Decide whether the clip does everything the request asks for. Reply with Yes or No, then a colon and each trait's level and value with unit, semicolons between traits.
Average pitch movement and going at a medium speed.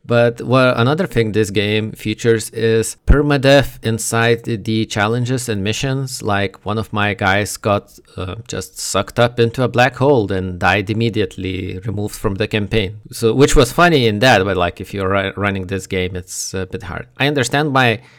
Yes: average, 3.6 semitones; average, 180 wpm